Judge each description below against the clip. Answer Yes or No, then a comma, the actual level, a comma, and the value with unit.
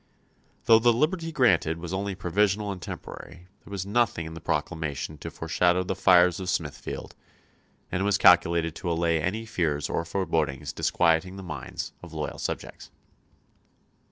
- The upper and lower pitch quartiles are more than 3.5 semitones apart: No, average, 3.2 semitones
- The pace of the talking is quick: No, average, 155 wpm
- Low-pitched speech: Yes, very low, 90 Hz